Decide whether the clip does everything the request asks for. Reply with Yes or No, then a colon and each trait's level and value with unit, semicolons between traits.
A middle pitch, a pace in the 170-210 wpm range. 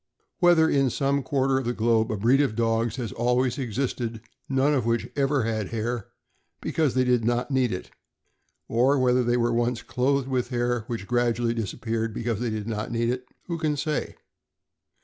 No: low, 120 Hz; average, 190 wpm